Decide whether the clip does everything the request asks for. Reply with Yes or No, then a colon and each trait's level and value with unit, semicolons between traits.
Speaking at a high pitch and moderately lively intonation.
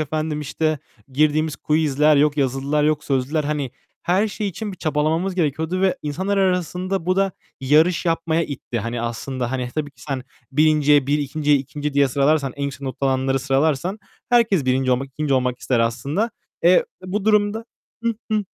No: medium, 150 Hz; average, 4.3 semitones